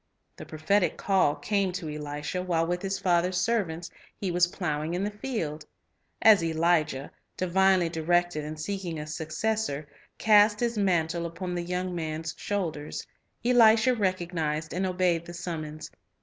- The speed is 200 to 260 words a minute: No, average, 145 wpm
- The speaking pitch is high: No, medium, 175 Hz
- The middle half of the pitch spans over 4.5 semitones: No, average, 3.4 semitones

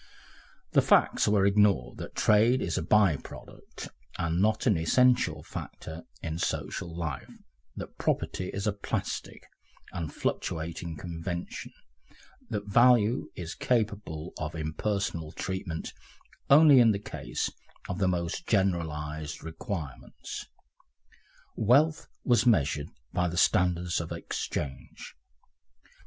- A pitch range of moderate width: Yes, average, 4.6 semitones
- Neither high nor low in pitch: No, very low, 90 Hz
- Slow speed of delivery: Yes, slow, 115 wpm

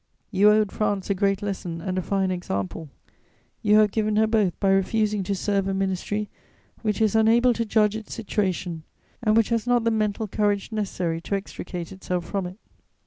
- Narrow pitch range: Yes, narrow, 2.3 semitones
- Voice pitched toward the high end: Yes, high, 205 Hz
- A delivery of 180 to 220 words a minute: Yes, average, 190 wpm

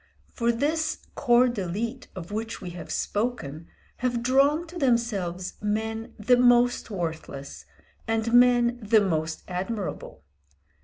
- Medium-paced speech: No, slow, 120 wpm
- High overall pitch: Yes, high, 225 Hz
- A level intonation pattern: No, average, 4.8 semitones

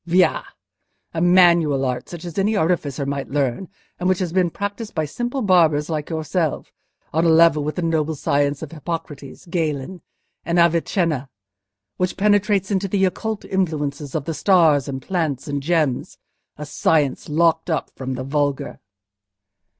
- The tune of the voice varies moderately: Yes, average, 3.8 semitones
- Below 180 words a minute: Yes, average, 150 wpm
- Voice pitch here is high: No, medium, 160 Hz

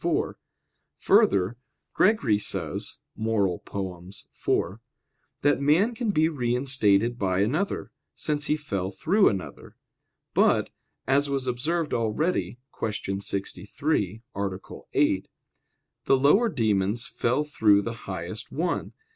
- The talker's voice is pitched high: No, low, 120 Hz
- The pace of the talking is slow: Yes, slow, 110 wpm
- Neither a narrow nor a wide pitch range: No, wide, 6.9 semitones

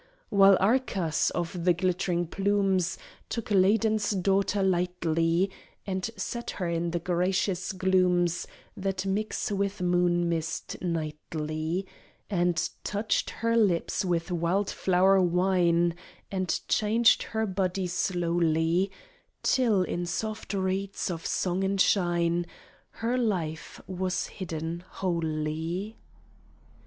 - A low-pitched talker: No, medium, 185 Hz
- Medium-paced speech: No, slow, 110 wpm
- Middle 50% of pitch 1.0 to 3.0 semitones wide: Yes, narrow, 2.4 semitones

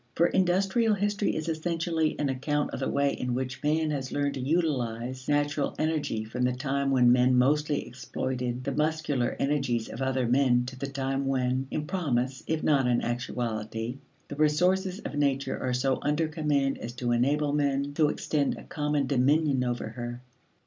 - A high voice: No, medium, 140 Hz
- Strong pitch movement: No, average, 3.1 semitones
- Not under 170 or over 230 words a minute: Yes, average, 175 wpm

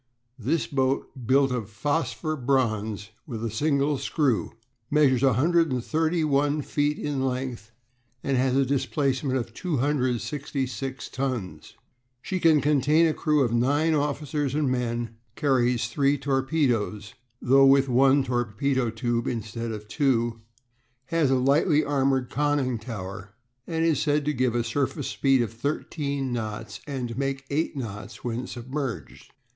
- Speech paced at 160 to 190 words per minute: No, slow, 135 wpm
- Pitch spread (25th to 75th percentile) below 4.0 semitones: Yes, average, 3.4 semitones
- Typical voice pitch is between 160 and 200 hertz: No, low, 135 Hz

